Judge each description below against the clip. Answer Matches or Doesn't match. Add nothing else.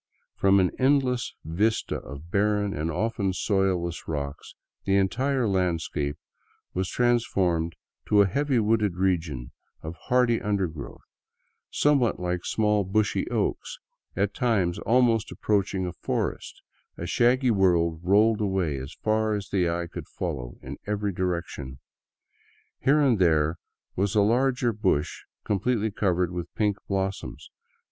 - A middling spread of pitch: Matches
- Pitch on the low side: Matches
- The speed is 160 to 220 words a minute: Doesn't match